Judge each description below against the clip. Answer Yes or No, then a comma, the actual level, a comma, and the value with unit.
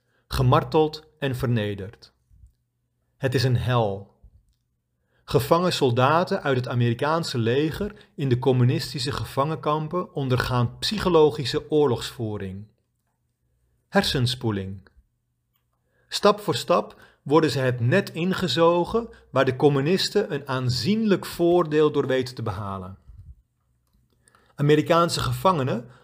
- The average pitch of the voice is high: No, low, 135 Hz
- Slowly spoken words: Yes, slow, 95 wpm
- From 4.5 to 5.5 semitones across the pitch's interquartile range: Yes, average, 5.2 semitones